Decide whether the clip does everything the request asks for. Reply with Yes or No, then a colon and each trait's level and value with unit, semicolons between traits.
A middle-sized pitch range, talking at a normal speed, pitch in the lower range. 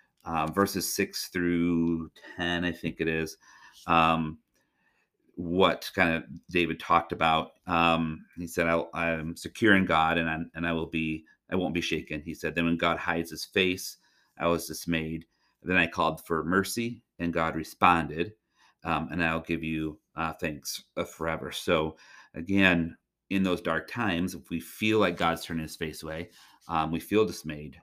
No: narrow, 1.4 semitones; average, 175 wpm; very low, 85 Hz